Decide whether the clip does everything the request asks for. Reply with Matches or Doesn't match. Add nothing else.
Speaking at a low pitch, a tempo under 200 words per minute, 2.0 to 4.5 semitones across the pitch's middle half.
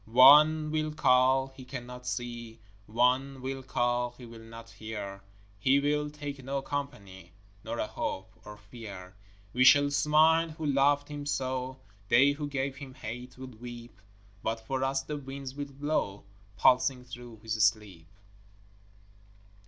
Matches